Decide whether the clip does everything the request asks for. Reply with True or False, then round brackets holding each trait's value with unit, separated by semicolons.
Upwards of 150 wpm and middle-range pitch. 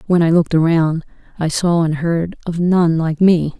True (200 wpm; 165 Hz)